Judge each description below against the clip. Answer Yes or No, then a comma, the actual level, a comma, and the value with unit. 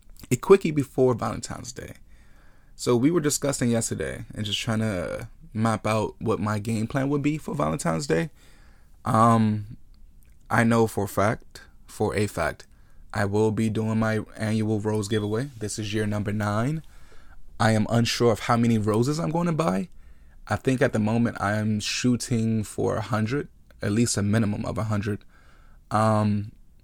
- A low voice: Yes, low, 110 Hz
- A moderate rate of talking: Yes, average, 170 wpm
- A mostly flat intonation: Yes, narrow, 2.3 semitones